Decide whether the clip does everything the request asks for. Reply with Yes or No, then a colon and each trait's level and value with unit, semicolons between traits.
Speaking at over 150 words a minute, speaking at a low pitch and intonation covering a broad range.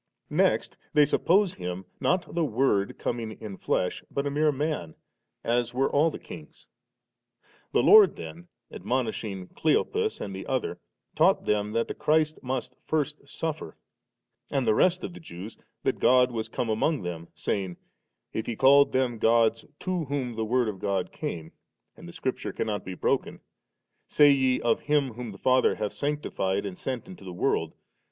Yes: average, 175 wpm; low, 125 Hz; wide, 6.1 semitones